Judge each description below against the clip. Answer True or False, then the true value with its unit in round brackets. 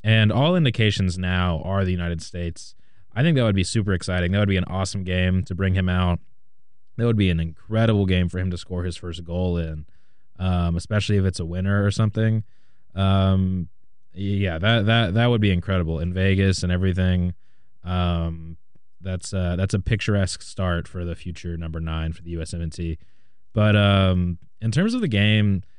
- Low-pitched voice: True (95 Hz)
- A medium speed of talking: True (190 wpm)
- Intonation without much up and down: False (3.0 semitones)